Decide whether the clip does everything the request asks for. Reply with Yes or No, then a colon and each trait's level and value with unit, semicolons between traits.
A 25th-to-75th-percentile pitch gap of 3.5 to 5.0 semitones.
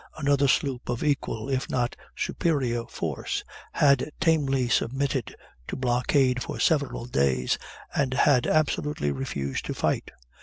No: average, 2.9 semitones